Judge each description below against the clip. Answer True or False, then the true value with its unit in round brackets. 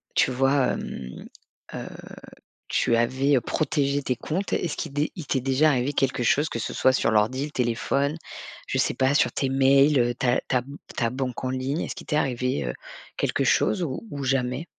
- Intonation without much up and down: True (2.3 semitones)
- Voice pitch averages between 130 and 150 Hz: True (135 Hz)